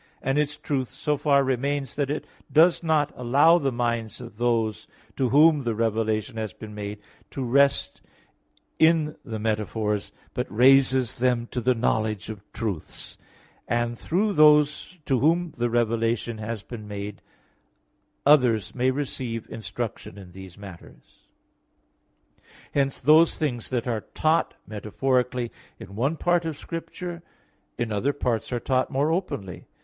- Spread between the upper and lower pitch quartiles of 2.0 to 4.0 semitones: No, average, 4.7 semitones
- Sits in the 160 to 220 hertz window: No, low, 125 Hz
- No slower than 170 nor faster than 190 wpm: No, average, 145 wpm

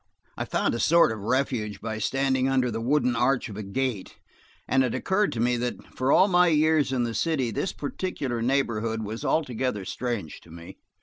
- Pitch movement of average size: Yes, average, 3.6 semitones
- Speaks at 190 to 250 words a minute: Yes, average, 195 wpm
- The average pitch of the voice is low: Yes, low, 125 Hz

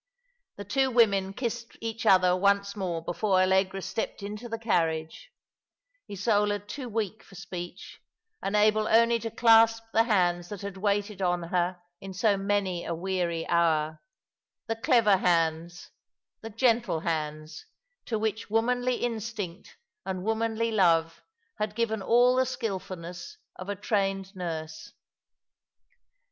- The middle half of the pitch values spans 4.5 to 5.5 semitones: No, average, 4.1 semitones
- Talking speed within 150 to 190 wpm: No, slow, 135 wpm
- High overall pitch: Yes, high, 200 Hz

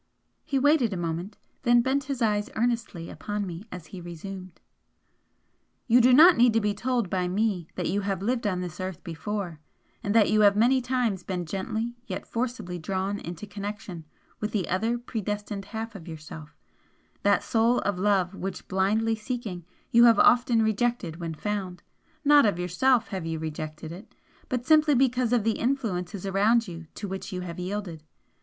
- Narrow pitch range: No, average, 4.6 semitones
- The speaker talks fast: No, average, 175 wpm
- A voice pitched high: Yes, high, 205 Hz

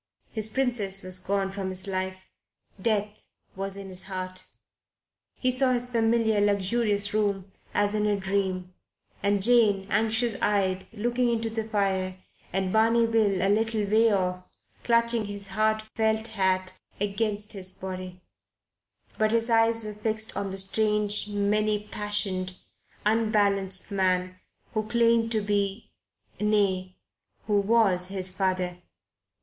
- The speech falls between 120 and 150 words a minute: Yes, slow, 135 wpm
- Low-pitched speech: No, high, 205 Hz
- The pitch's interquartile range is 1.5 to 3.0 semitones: Yes, narrow, 2.5 semitones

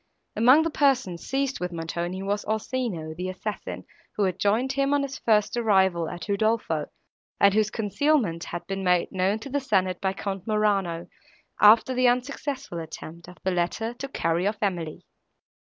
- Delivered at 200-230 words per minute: No, average, 170 wpm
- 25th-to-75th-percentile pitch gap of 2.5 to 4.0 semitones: No, average, 5.3 semitones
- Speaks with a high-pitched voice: Yes, high, 200 Hz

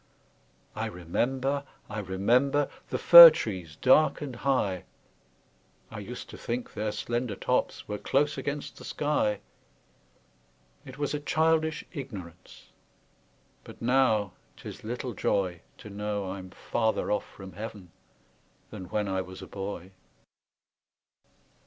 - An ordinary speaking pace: No, slow, 125 wpm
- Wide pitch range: Yes, wide, 6.0 semitones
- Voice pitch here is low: Yes, low, 110 Hz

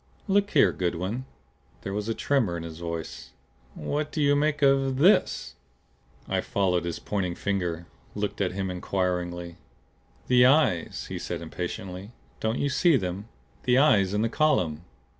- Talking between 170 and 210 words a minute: No, average, 155 wpm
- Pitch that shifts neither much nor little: No, wide, 7.4 semitones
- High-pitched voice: No, low, 100 Hz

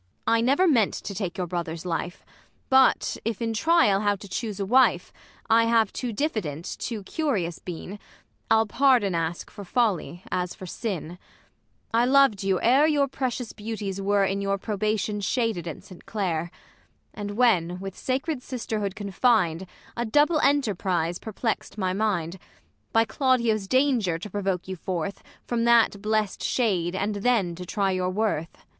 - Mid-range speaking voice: No, high, 205 Hz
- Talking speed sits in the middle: Yes, average, 160 wpm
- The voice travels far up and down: No, average, 4.3 semitones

